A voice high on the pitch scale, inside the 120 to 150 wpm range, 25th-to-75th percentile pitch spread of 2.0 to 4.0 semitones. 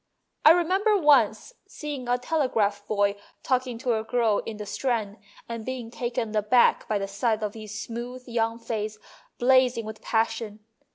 No: high, 230 Hz; average, 160 wpm; average, 2.9 semitones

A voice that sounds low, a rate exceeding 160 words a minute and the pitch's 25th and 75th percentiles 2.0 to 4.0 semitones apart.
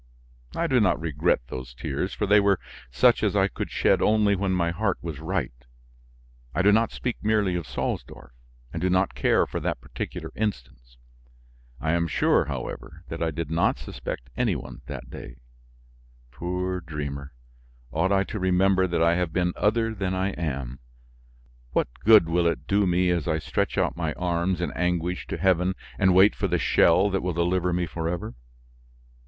Yes: very low, 90 Hz; average, 180 wpm; average, 2.8 semitones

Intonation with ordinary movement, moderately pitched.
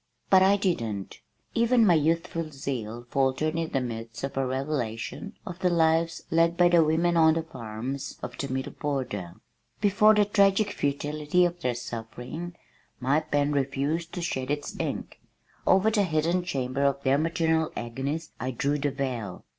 Yes: average, 4.5 semitones; medium, 150 Hz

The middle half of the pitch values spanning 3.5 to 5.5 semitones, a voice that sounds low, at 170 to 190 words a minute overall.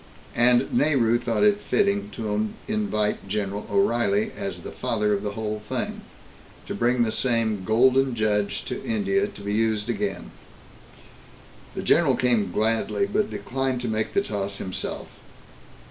No: average, 4.2 semitones; low, 115 Hz; average, 145 wpm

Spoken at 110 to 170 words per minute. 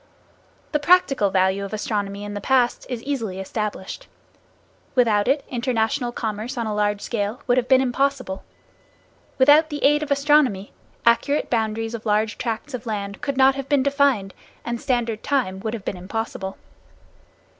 Yes: average, 160 wpm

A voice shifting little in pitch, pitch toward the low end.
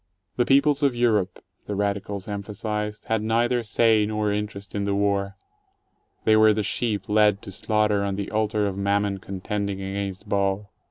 Yes: narrow, 1.4 semitones; low, 105 Hz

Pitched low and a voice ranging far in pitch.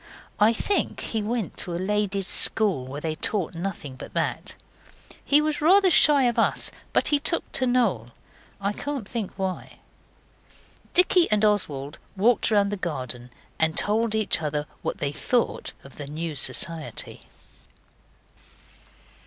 No: high, 200 Hz; wide, 7.1 semitones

